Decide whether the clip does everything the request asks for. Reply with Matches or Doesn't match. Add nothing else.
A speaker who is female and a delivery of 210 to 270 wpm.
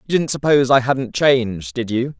Doesn't match